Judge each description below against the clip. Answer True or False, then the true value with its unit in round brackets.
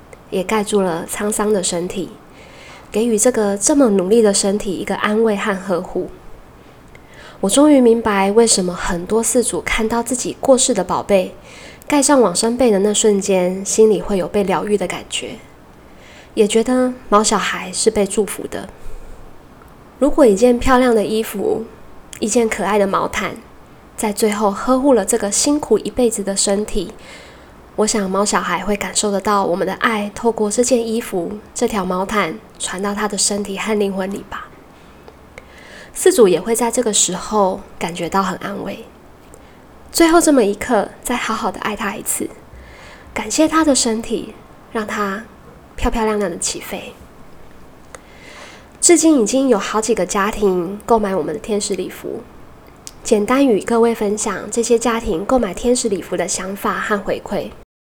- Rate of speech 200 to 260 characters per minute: True (240 characters per minute)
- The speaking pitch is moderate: False (210 Hz)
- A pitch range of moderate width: True (3.0 semitones)